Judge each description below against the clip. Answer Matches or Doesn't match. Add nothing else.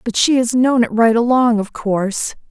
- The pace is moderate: Doesn't match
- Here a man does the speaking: Doesn't match